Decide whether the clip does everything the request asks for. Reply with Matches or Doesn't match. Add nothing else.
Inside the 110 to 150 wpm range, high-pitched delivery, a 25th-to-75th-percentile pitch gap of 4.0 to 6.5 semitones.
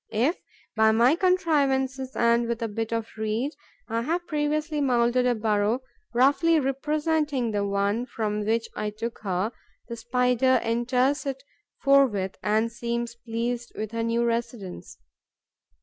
Doesn't match